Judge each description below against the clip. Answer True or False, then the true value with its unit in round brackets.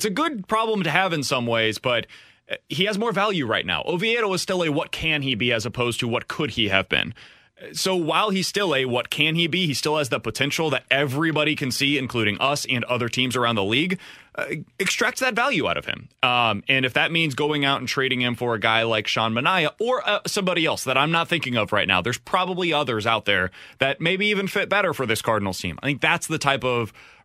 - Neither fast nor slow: False (245 wpm)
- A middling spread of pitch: False (6.7 semitones)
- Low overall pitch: False (145 Hz)